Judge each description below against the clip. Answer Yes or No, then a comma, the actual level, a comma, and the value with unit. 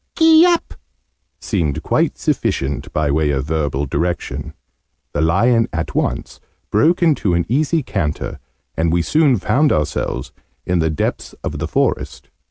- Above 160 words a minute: No, average, 145 wpm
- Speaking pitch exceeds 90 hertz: No, very low, 85 Hz